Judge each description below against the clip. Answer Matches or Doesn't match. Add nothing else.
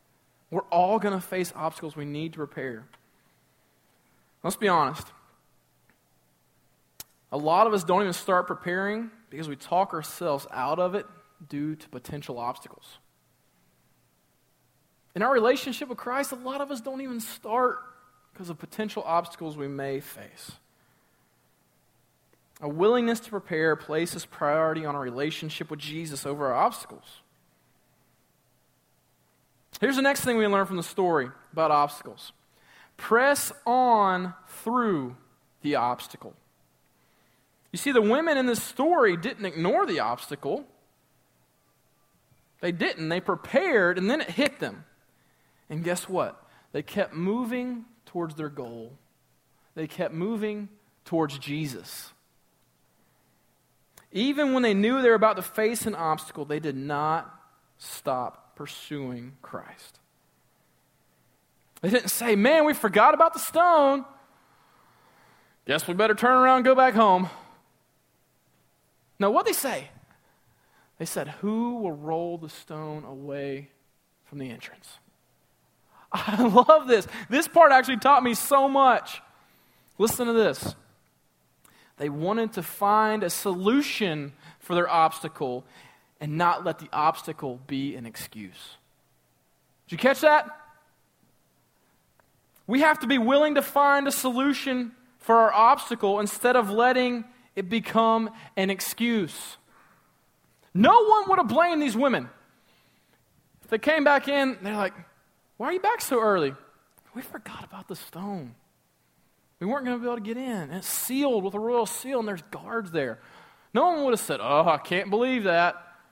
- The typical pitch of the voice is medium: Doesn't match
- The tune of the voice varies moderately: Doesn't match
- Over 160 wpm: Doesn't match